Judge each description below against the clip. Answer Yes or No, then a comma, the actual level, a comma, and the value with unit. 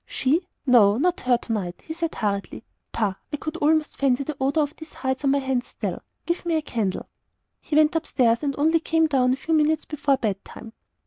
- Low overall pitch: No, very high, 280 Hz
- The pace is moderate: No, fast, 220 wpm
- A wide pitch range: No, average, 4.3 semitones